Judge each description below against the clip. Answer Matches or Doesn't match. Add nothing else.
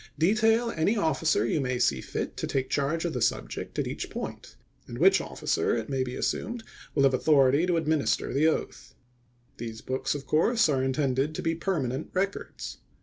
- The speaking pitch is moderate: Matches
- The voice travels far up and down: Doesn't match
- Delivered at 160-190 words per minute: Matches